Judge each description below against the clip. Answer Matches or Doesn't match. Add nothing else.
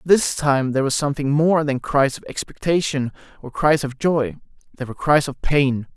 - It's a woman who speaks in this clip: Doesn't match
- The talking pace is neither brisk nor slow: Matches